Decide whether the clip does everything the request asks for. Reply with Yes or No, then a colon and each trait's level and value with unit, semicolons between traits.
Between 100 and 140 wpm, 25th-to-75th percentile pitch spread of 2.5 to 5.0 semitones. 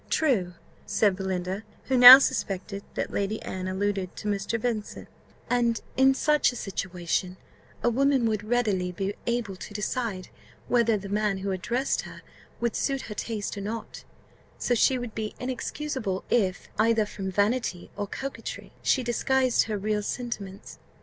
No: average, 155 wpm; average, 3.8 semitones